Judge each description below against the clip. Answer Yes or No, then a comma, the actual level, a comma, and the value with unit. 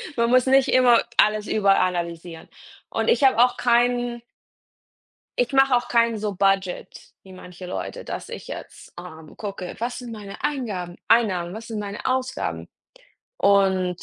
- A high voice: Yes, high, 215 Hz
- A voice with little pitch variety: No, average, 4.9 semitones